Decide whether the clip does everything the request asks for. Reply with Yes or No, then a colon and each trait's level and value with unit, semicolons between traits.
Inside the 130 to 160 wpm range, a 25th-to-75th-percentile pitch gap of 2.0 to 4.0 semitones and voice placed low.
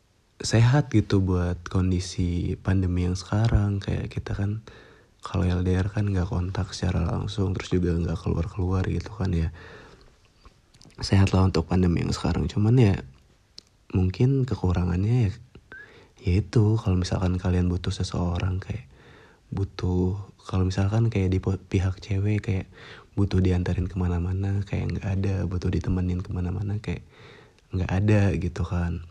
Yes: average, 135 wpm; narrow, 2.4 semitones; very low, 95 Hz